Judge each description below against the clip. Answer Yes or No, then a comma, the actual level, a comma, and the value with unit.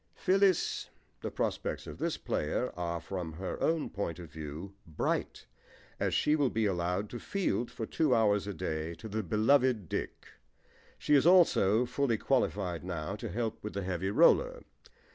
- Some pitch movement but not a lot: No, wide, 6.9 semitones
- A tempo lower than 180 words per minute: Yes, average, 165 wpm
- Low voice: Yes, low, 105 Hz